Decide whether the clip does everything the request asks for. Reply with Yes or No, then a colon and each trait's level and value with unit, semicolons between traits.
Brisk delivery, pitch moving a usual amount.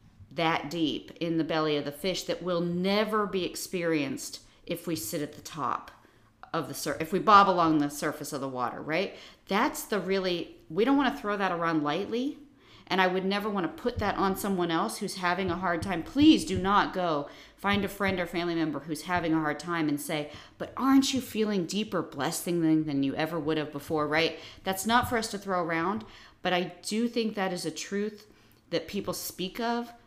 Yes: fast, 210 wpm; average, 4.1 semitones